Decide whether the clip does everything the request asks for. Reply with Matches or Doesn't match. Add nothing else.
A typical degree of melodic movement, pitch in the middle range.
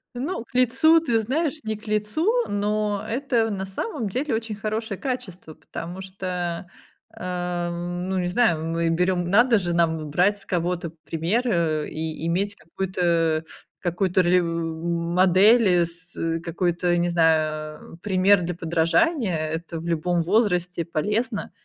Matches